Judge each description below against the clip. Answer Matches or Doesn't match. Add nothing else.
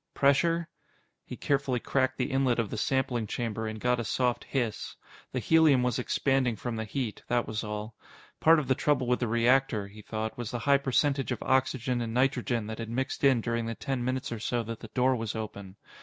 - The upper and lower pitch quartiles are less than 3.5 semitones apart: Matches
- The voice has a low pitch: Matches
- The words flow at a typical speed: Doesn't match